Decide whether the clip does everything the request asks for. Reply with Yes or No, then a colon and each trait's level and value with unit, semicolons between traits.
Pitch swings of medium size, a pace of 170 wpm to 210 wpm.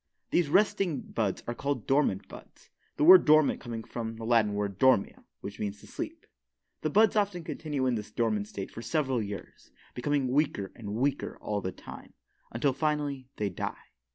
No: wide, 6.0 semitones; average, 180 wpm